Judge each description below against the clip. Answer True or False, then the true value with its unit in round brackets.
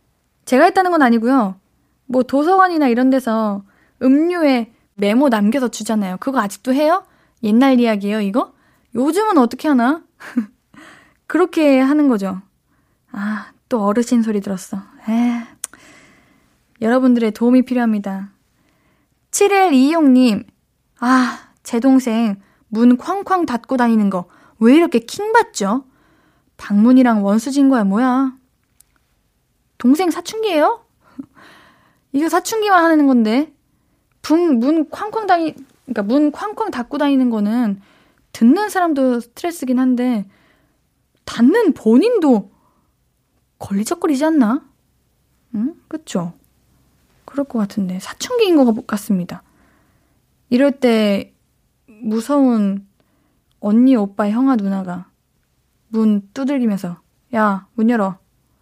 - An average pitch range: True (4.9 semitones)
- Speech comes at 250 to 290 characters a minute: False (230 characters per minute)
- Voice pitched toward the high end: True (250 Hz)